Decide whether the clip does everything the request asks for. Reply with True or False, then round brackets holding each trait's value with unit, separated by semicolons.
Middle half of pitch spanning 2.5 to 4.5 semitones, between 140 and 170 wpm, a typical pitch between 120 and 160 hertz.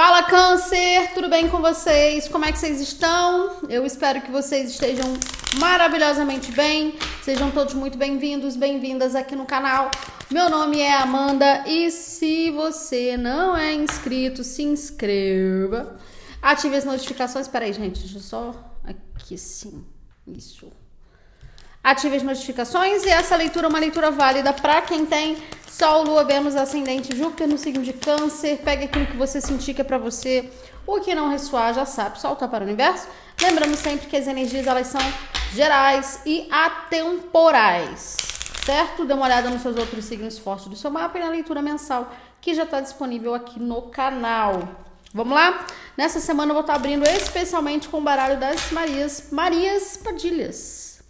False (3.4 semitones; 165 wpm; 285 Hz)